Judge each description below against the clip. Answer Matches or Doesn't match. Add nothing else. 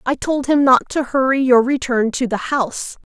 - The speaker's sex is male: Doesn't match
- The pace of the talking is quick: Matches